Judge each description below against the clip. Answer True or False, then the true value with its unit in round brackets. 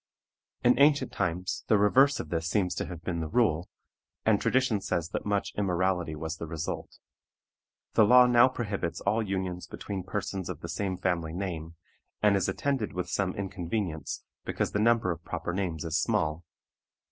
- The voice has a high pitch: False (95 Hz)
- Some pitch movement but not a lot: True (3.9 semitones)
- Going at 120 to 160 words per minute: False (170 wpm)